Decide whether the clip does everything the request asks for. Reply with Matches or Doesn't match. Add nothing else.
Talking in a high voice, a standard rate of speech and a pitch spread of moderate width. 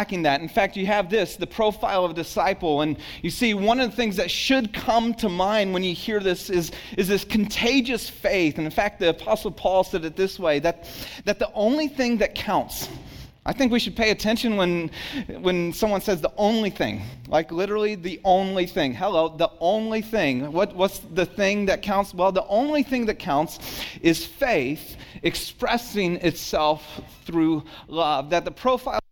Matches